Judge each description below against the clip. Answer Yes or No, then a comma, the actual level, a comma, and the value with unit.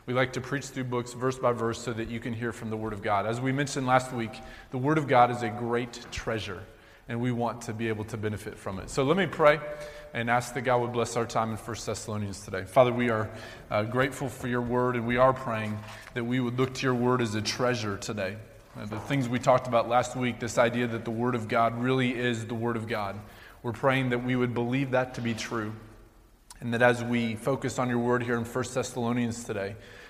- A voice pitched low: Yes, low, 120 Hz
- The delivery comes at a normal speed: No, fast, 250 wpm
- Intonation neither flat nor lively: No, narrow, 2.2 semitones